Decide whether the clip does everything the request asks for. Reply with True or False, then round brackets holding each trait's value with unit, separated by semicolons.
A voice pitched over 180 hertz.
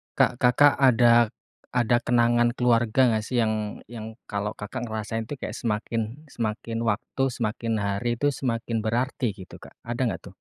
False (115 Hz)